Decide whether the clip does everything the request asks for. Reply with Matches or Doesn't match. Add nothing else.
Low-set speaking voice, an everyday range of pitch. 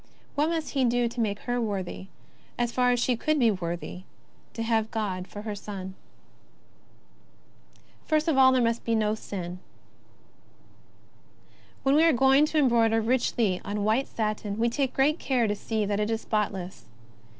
Doesn't match